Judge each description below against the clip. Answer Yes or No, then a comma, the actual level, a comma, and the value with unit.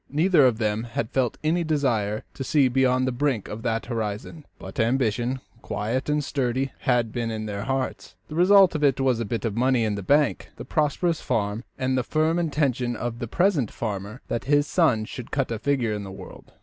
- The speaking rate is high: Yes, fast, 210 wpm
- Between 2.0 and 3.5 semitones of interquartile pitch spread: No, average, 4.3 semitones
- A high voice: No, low, 125 Hz